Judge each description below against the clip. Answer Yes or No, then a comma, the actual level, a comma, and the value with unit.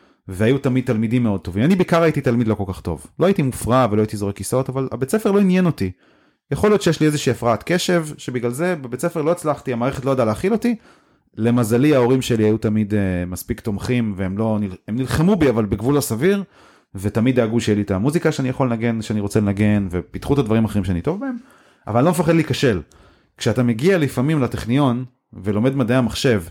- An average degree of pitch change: No, wide, 5.7 semitones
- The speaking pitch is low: Yes, low, 125 Hz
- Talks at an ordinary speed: No, fast, 200 wpm